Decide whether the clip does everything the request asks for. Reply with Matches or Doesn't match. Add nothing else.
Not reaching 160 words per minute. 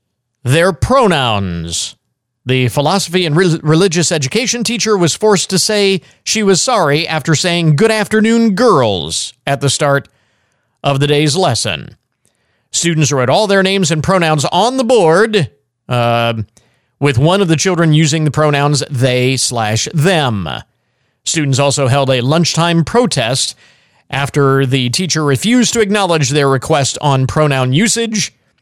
Matches